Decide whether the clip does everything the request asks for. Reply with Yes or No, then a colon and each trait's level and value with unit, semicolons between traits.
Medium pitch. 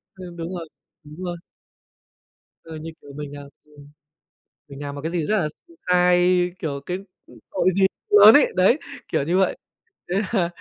Yes: medium, 175 Hz